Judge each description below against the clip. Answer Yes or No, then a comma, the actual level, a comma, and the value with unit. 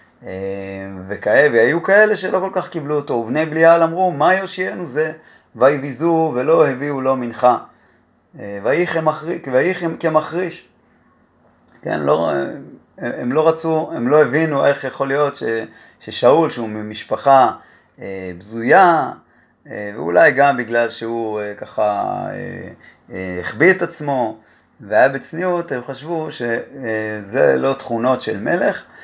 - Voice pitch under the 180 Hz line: Yes, medium, 140 Hz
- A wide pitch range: Yes, wide, 6.2 semitones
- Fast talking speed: No, average, 110 wpm